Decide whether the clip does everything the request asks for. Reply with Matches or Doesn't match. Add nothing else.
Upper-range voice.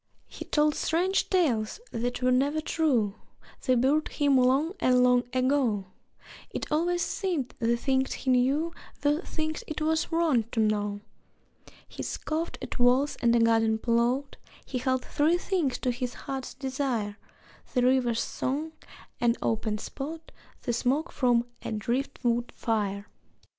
Matches